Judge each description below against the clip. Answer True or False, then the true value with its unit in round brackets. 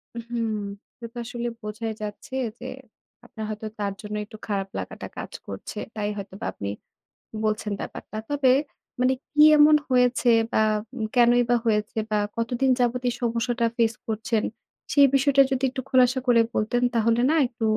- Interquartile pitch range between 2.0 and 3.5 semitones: True (2.5 semitones)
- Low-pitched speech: False (235 Hz)